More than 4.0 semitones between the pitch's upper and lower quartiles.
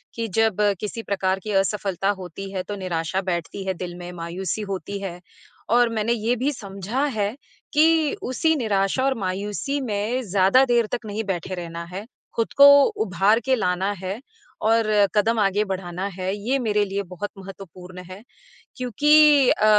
No: average, 3.5 semitones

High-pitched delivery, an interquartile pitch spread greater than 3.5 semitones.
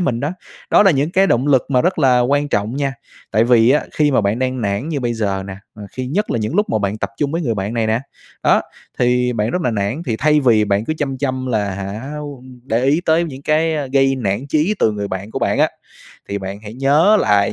No: low, 125 Hz; average, 5.1 semitones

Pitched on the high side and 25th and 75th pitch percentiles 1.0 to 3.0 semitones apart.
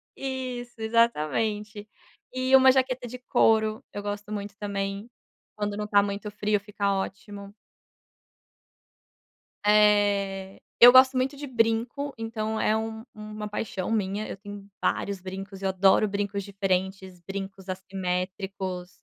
Yes: high, 205 Hz; narrow, 2.4 semitones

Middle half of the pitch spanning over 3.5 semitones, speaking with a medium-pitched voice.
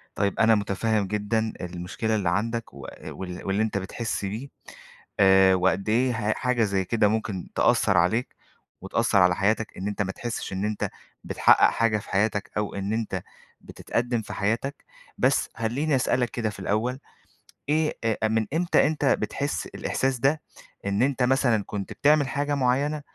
No: average, 3.9 semitones; low, 110 Hz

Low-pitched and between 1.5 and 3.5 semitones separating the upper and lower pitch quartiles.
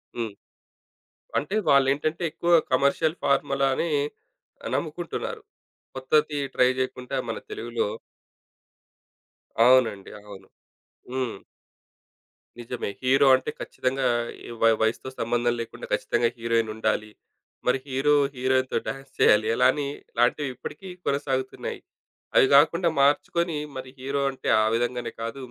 Yes: low, 130 Hz; average, 2.8 semitones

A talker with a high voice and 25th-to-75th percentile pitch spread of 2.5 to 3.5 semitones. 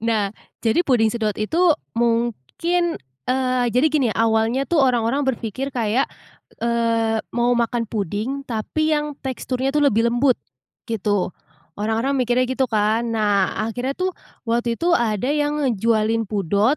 Yes: high, 235 Hz; average, 3.2 semitones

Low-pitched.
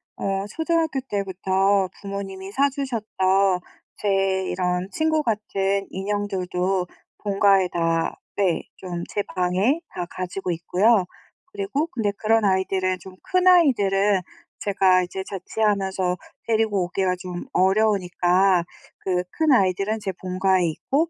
No: high, 195 Hz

